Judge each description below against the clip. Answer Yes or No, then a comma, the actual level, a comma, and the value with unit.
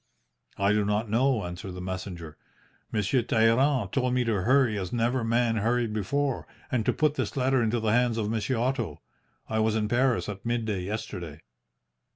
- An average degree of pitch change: Yes, average, 3.2 semitones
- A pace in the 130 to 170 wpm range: No, average, 180 wpm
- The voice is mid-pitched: No, low, 115 Hz